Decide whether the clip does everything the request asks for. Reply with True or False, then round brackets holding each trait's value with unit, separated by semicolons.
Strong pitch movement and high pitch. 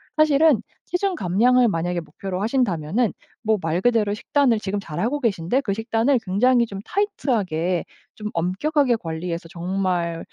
True (6.1 semitones; 210 Hz)